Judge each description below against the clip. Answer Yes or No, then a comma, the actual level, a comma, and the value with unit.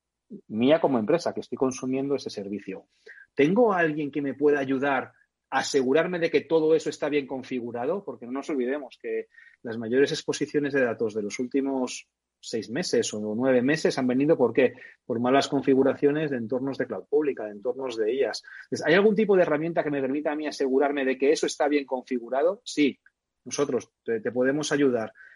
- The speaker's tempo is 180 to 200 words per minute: Yes, average, 185 wpm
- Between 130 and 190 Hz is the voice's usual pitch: Yes, medium, 140 Hz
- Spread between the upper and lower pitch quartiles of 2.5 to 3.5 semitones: Yes, average, 3.1 semitones